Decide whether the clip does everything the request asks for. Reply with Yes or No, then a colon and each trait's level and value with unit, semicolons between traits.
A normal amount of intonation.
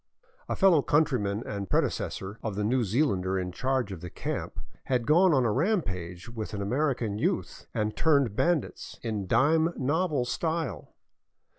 No: wide, 7.1 semitones